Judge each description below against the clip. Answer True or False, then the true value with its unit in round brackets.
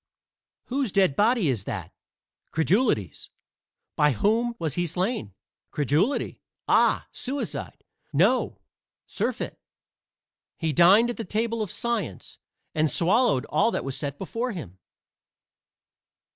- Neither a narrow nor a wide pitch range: False (8.1 semitones)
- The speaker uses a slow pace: True (115 wpm)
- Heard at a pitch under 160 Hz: False (185 Hz)